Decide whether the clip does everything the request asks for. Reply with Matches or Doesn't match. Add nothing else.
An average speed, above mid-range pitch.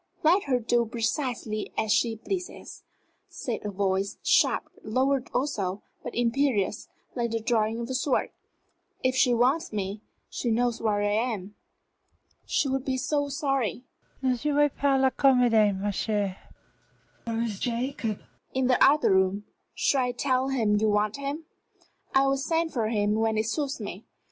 Matches